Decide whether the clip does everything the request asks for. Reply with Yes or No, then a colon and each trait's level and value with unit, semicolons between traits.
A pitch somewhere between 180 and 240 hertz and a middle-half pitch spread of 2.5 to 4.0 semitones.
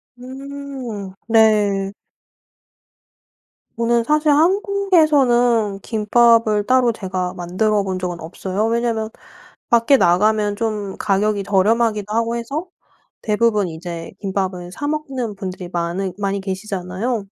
Yes: high, 215 Hz; average, 3.7 semitones